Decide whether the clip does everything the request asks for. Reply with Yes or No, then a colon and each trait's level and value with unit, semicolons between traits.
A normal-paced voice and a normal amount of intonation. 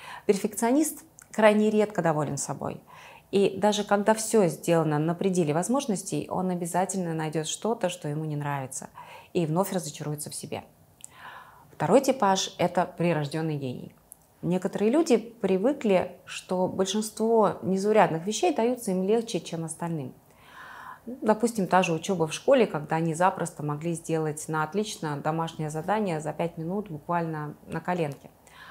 Yes: average, 135 wpm; average, 4.9 semitones